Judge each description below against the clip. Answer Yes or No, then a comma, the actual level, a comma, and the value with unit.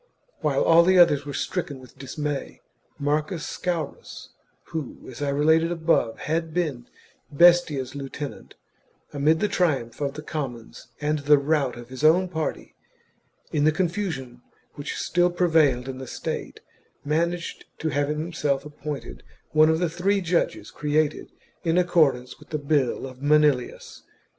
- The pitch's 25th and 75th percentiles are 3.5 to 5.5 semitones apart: No, average, 3.1 semitones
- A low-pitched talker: No, medium, 150 Hz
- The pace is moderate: Yes, average, 145 wpm